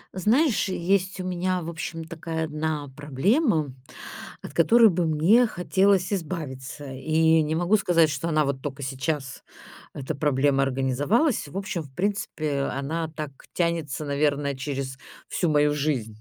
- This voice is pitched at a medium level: Yes, medium, 155 Hz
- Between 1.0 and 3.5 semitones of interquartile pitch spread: No, average, 4.2 semitones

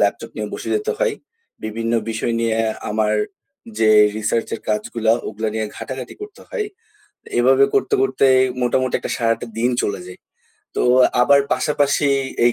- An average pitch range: Yes, average, 4.2 semitones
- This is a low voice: Yes, low, 120 Hz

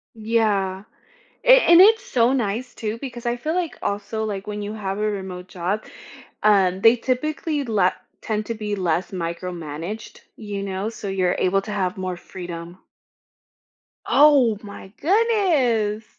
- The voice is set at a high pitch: Yes, high, 210 Hz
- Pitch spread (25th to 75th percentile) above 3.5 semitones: Yes, average, 4.2 semitones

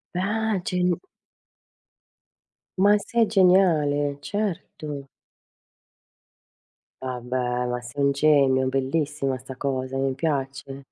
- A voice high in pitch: No, medium, 140 Hz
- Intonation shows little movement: No, average, 5.2 semitones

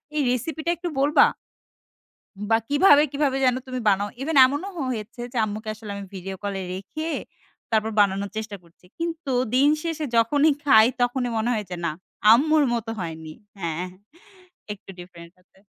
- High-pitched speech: Yes, high, 230 Hz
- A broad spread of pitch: Yes, wide, 6.4 semitones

